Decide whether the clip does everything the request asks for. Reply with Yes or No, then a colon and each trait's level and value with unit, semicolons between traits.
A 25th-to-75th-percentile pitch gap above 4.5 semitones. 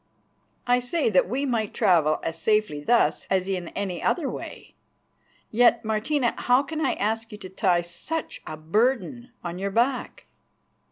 Yes: average, 5.2 semitones